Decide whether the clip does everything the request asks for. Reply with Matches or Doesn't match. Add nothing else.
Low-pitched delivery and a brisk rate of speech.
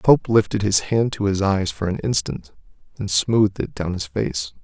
Matches